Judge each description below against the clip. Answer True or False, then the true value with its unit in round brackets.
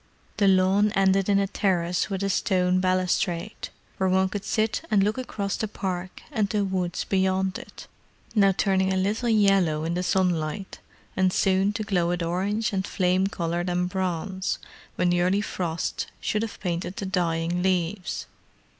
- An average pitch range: False (1.8 semitones)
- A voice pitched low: False (190 Hz)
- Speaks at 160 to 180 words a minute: True (165 wpm)